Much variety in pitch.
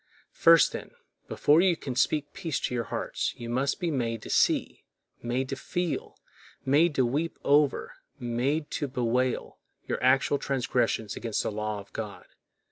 No: average, 3.8 semitones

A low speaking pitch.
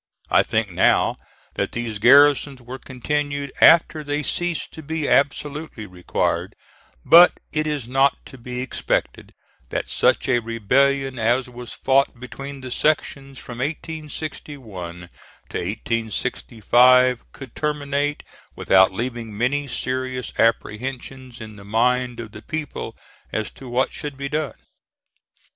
Yes: low, 130 Hz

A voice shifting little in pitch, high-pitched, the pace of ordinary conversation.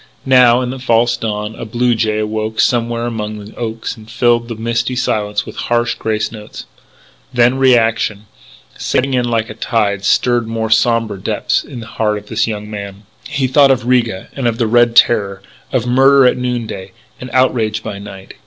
No: narrow, 2.2 semitones; low, 115 Hz; average, 190 wpm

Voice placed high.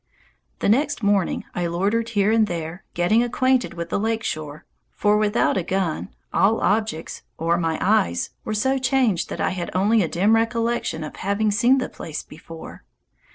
Yes: high, 205 Hz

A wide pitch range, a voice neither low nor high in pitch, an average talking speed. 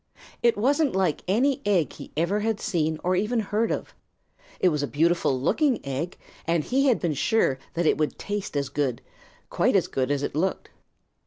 Yes: wide, 6.7 semitones; medium, 180 Hz; average, 190 wpm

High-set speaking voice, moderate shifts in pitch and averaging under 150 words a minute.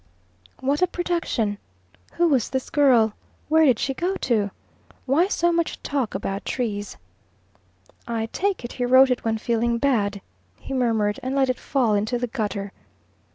No: very high, 250 Hz; average, 4.2 semitones; average, 160 wpm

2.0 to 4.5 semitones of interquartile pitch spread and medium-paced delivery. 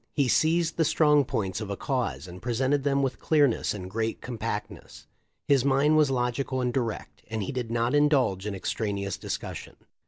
Yes: average, 4.2 semitones; average, 180 wpm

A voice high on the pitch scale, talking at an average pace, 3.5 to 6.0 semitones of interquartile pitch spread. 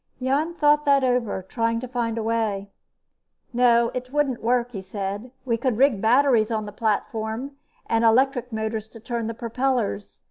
No: high, 235 Hz; average, 170 wpm; average, 2.7 semitones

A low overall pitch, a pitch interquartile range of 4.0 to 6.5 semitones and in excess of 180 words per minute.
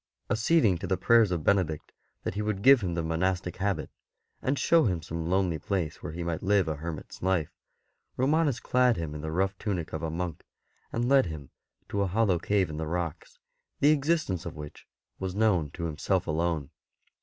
Yes: very low, 90 Hz; average, 4.5 semitones; average, 200 wpm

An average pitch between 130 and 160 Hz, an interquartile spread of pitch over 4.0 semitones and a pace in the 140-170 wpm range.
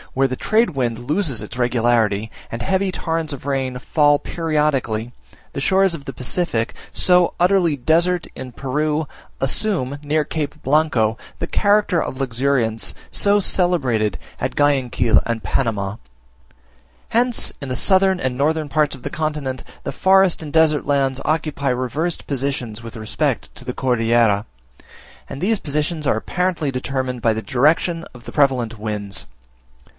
Yes: medium, 140 Hz; average, 5.0 semitones; average, 150 wpm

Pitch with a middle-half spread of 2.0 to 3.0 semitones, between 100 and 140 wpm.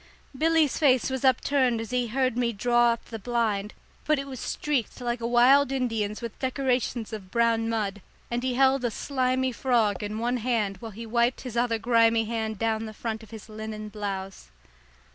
No: narrow, 2.6 semitones; average, 190 wpm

